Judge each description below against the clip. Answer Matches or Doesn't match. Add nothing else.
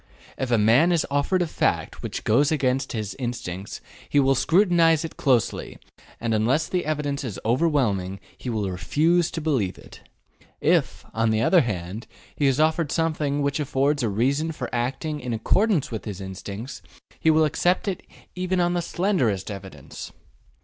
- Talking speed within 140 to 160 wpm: Doesn't match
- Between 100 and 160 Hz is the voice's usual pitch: Matches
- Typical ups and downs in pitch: Doesn't match